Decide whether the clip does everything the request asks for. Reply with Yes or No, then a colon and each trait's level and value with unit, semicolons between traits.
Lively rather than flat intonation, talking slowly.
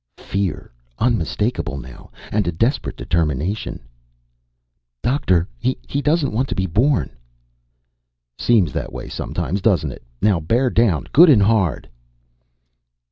Yes: wide, 6.7 semitones; slow, 120 wpm